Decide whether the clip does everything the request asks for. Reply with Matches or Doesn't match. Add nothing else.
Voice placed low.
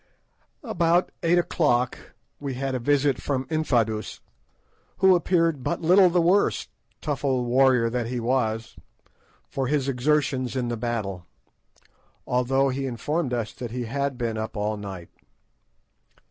Matches